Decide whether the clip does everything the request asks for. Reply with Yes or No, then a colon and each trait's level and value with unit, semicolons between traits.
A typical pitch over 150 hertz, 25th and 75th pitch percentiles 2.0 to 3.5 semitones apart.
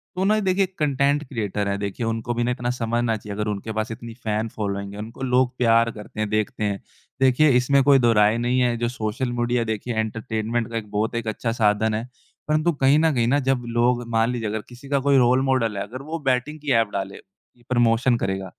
No: low, 120 Hz; average, 3.0 semitones